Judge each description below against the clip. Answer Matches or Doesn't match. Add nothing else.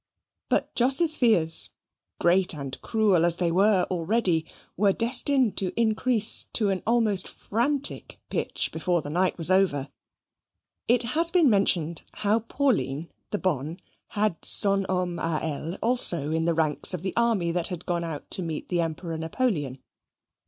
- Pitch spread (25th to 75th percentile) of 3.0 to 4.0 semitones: Doesn't match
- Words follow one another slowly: Doesn't match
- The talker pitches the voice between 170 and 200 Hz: Matches